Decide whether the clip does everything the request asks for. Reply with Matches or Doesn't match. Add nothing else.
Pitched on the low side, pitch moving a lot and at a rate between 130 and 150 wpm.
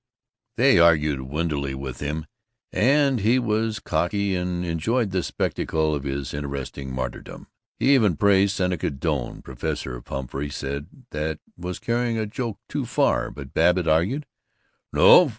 Matches